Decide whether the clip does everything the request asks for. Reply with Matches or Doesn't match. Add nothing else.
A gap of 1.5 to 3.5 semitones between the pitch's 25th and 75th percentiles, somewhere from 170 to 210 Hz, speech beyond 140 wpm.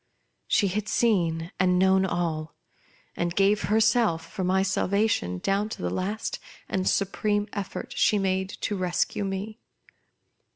Doesn't match